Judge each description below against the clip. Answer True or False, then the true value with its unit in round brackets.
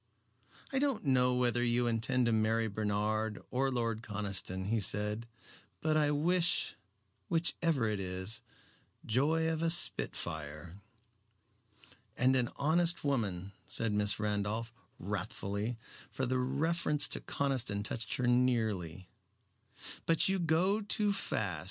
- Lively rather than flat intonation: True (6.1 semitones)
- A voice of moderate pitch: False (120 Hz)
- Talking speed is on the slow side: True (125 wpm)